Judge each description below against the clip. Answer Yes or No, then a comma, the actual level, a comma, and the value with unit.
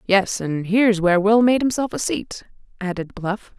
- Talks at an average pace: Yes, average, 185 wpm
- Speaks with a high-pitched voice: Yes, high, 205 Hz